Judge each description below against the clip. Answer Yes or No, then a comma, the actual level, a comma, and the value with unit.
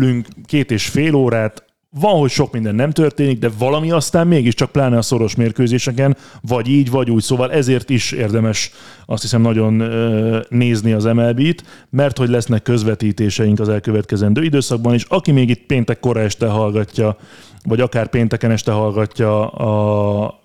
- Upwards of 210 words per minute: No, fast, 155 wpm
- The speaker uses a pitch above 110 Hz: Yes, low, 120 Hz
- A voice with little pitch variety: No, average, 3.3 semitones